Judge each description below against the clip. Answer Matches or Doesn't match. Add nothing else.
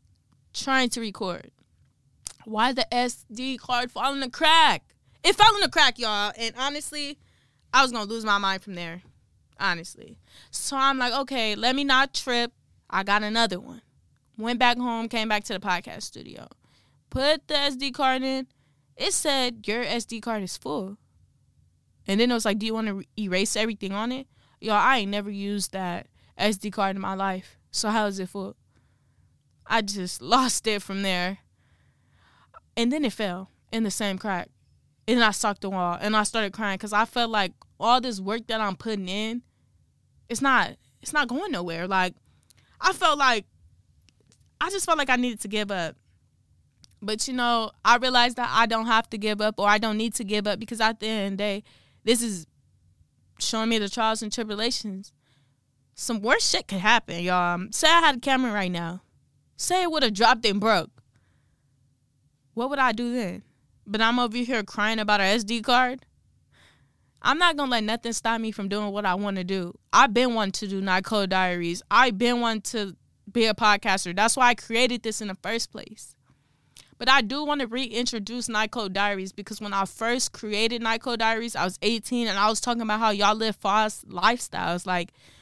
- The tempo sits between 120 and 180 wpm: Doesn't match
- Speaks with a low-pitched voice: Doesn't match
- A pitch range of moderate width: Matches